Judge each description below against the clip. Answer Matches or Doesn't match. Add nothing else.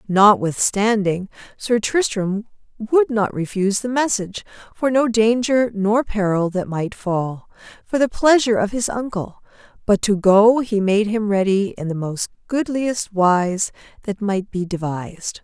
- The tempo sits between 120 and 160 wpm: Matches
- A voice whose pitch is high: Matches